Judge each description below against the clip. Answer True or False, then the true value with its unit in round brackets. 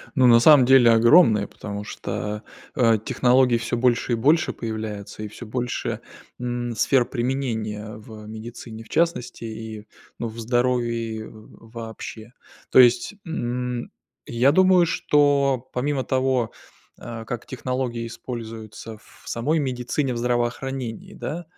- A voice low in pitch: True (120 Hz)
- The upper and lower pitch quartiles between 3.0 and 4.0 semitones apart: False (2.6 semitones)